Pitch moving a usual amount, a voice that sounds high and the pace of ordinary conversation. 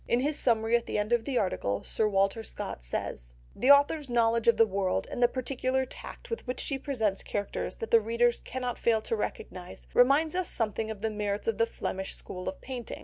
No: average, 3.6 semitones; high, 230 Hz; fast, 215 wpm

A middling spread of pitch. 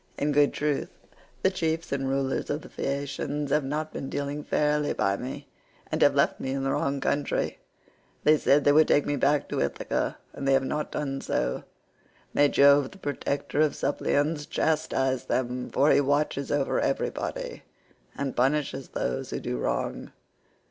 No: narrow, 1.6 semitones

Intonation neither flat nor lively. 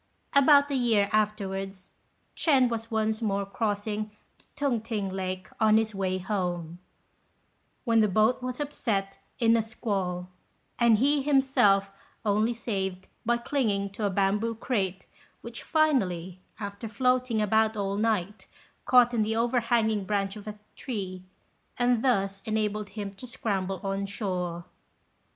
Yes: average, 3.2 semitones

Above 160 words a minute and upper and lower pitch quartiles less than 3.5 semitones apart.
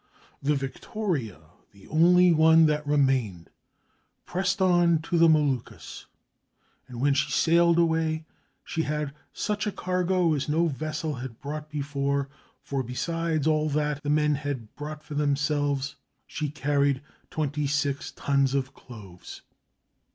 No: slow, 135 wpm; average, 2.7 semitones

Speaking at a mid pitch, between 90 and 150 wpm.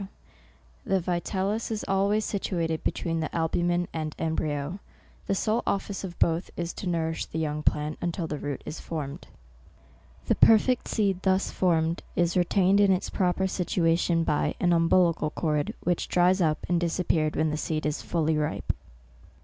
No: medium, 170 Hz; average, 165 wpm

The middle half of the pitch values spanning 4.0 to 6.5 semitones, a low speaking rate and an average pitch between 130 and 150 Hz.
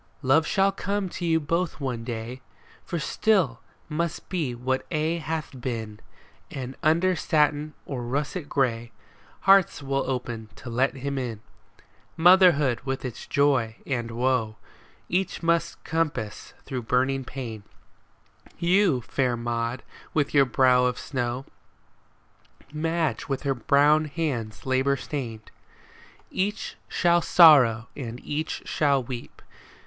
Yes: average, 4.7 semitones; slow, 130 wpm; low, 135 Hz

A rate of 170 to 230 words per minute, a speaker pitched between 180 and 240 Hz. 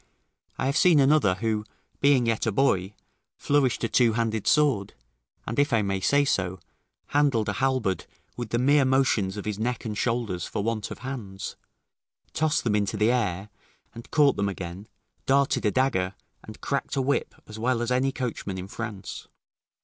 No: average, 180 wpm; low, 115 Hz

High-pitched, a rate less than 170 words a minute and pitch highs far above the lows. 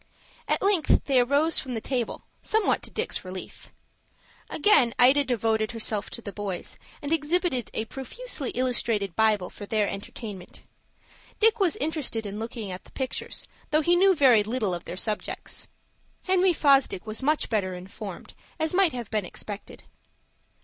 Yes: high, 245 Hz; average, 155 wpm; wide, 6.4 semitones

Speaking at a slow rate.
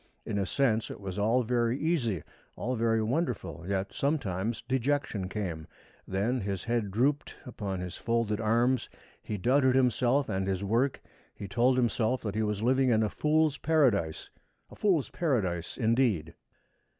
No: average, 155 wpm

